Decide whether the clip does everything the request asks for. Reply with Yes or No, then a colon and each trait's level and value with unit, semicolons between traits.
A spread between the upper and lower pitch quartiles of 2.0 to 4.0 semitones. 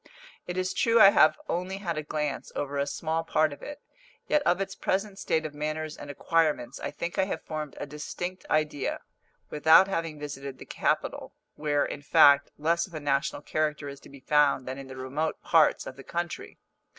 Yes: average, 3.0 semitones